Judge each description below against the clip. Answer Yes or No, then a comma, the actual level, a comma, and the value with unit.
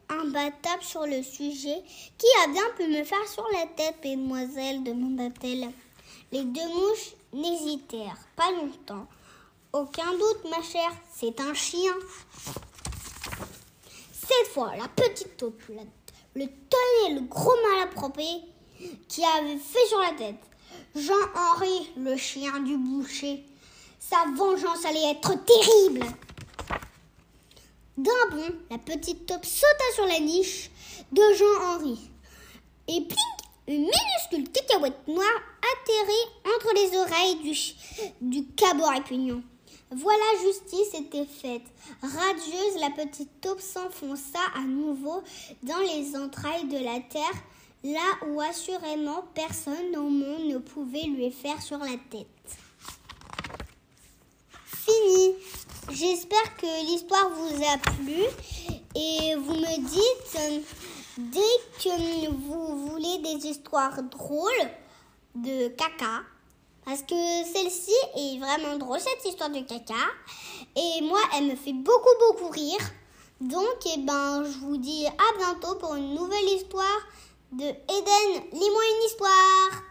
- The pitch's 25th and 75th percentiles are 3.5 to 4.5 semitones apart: No, average, 5.3 semitones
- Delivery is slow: Yes, slow, 125 wpm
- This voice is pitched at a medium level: No, very high, 320 Hz